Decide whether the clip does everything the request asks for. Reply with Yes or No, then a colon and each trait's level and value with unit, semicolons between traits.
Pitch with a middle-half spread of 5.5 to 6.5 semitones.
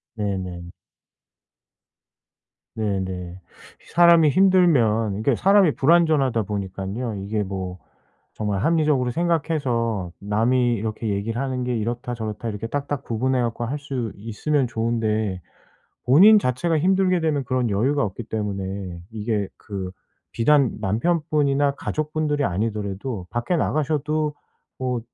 Yes: wide, 6.0 semitones